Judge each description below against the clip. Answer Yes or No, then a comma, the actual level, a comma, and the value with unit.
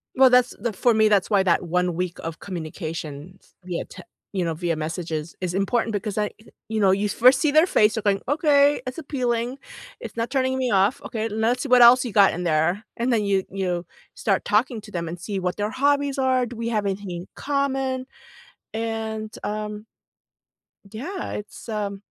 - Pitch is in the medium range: No, high, 215 Hz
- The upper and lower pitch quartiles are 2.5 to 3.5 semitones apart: No, average, 5.2 semitones